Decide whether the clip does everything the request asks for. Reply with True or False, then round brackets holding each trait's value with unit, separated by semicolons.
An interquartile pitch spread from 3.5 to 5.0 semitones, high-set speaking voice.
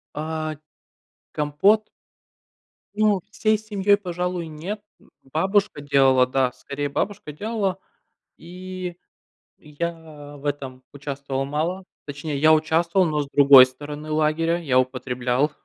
False (4.3 semitones; 155 Hz)